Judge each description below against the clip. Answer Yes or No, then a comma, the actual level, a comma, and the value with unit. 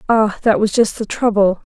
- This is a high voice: Yes, high, 210 Hz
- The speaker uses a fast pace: Yes, fast, 210 wpm